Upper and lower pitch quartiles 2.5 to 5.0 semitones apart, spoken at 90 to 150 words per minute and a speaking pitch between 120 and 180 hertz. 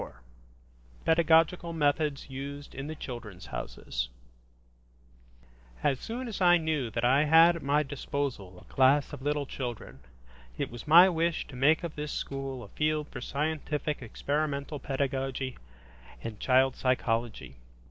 Yes: average, 3.9 semitones; average, 145 wpm; medium, 140 Hz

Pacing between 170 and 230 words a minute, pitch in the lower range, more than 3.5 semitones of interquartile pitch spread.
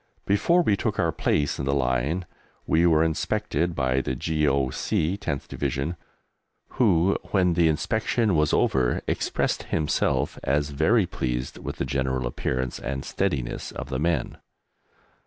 No: average, 140 wpm; very low, 75 Hz; average, 4.7 semitones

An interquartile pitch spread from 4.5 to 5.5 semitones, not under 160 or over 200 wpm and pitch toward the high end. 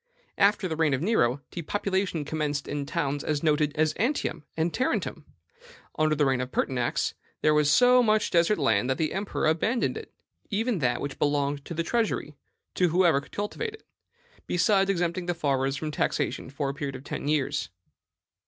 No: average, 5.1 semitones; average, 180 wpm; medium, 155 Hz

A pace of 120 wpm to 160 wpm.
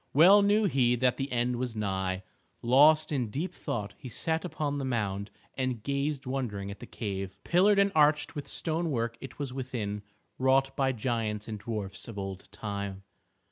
No: average, 180 wpm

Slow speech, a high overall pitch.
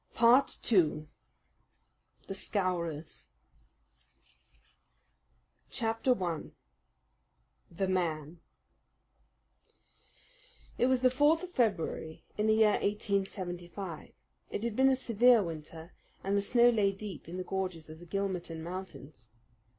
Yes: slow, 110 wpm; high, 195 Hz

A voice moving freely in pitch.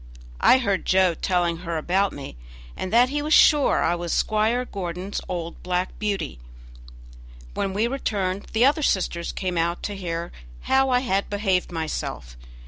No: average, 4.3 semitones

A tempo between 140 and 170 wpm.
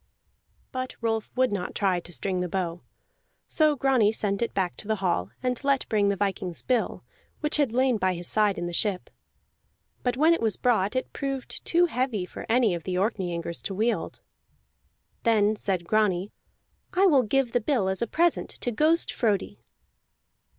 No: average, 180 wpm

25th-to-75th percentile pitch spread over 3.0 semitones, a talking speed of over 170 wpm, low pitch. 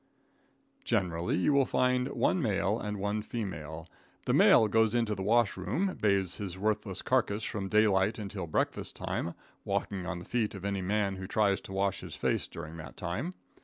No: average, 2.7 semitones; average, 180 wpm; low, 100 Hz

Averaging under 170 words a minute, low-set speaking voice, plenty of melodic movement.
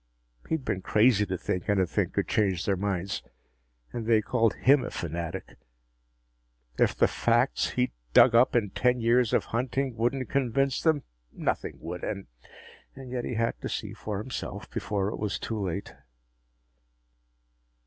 No: average, 150 wpm; low, 115 Hz; average, 4.2 semitones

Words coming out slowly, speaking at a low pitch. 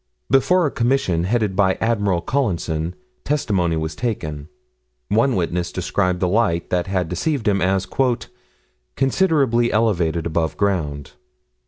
Yes: slow, 125 wpm; very low, 95 Hz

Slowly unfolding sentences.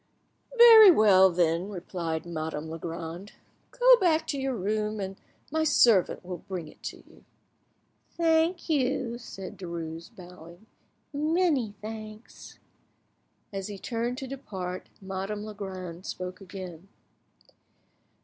Yes: slow, 110 wpm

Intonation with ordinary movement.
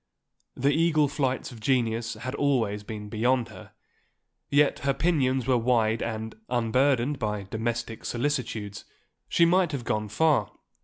Yes: average, 4.0 semitones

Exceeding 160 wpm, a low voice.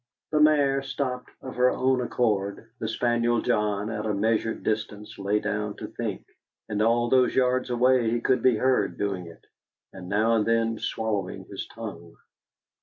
Yes: average, 170 wpm; low, 115 Hz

